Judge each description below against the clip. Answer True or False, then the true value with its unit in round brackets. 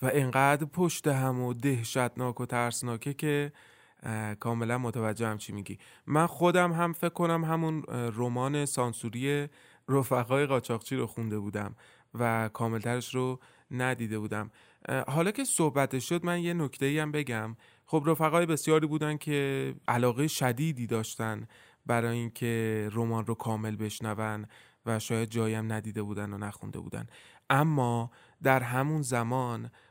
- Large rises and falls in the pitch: False (4.2 semitones)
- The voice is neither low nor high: False (125 Hz)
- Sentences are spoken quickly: False (135 wpm)